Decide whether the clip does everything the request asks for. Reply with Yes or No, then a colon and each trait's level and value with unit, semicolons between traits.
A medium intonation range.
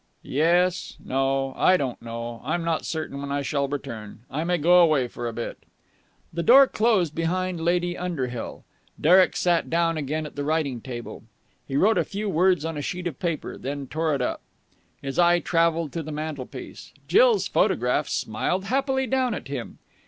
Yes: average, 4.5 semitones